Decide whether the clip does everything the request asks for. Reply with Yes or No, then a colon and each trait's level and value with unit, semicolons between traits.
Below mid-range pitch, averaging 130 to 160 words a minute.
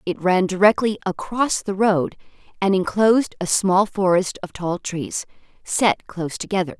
No: high, 190 Hz; average, 150 wpm